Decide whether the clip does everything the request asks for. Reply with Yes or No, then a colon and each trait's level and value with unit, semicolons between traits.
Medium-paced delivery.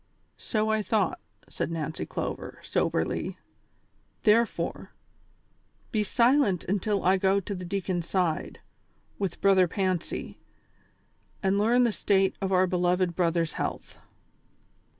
No: slow, 125 wpm